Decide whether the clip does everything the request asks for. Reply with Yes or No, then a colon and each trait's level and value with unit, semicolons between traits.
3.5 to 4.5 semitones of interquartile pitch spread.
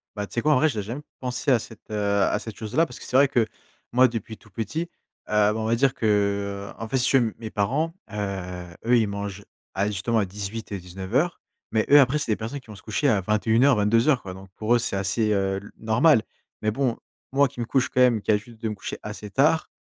Yes: average, 3.8 semitones